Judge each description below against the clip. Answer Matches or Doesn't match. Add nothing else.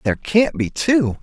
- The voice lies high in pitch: Doesn't match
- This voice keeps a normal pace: Matches